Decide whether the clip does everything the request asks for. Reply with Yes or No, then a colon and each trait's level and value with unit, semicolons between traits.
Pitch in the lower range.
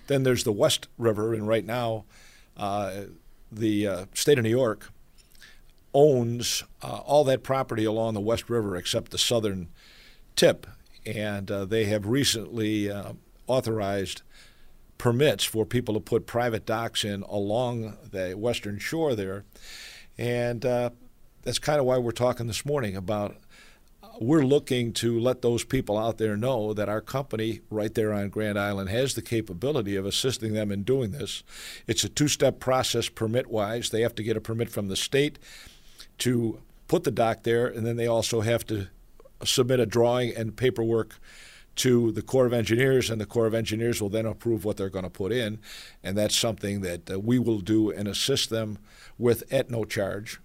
Yes: low, 115 Hz